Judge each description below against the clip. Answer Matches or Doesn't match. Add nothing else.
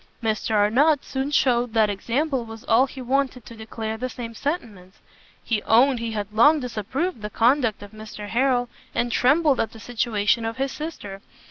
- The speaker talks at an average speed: Matches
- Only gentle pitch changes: Doesn't match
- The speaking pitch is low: Doesn't match